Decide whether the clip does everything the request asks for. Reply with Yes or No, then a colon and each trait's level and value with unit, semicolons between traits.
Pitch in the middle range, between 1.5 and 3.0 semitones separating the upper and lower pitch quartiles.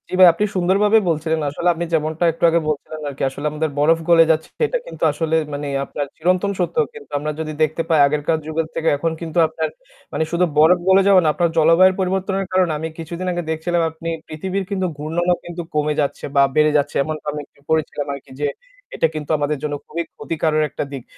Yes: medium, 160 Hz; average, 2.7 semitones